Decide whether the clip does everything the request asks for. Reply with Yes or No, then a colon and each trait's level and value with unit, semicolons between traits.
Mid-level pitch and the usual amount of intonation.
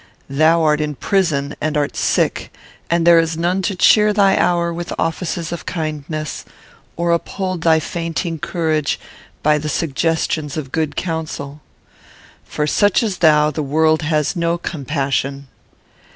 No: medium, 160 Hz; narrow, 2.2 semitones